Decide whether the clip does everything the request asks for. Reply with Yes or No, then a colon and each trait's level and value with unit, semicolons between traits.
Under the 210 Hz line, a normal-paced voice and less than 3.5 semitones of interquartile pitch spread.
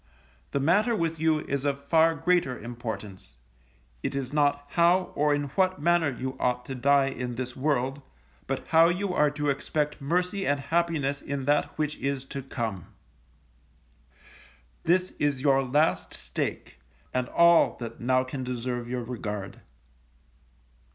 No: medium, 140 Hz; average, 150 wpm; average, 4.1 semitones